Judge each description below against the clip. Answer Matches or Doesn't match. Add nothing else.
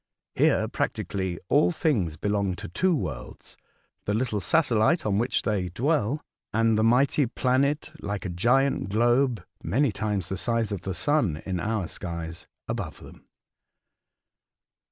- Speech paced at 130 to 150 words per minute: Matches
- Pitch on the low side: Matches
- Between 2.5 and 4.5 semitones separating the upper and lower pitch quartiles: Doesn't match